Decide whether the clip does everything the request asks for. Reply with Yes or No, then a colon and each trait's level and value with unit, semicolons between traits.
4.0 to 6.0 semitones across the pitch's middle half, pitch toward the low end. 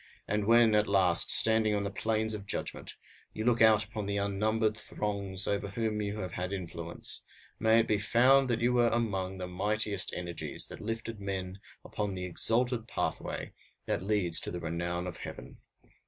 No: average, 2.8 semitones; low, 105 Hz